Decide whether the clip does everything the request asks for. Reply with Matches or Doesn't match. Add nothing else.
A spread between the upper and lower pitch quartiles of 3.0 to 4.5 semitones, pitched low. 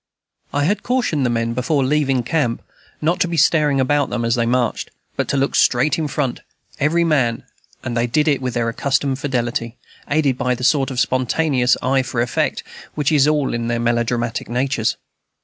Matches